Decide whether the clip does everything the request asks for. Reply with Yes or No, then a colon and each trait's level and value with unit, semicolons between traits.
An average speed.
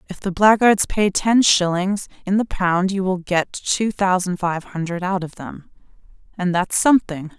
Yes: average, 180 wpm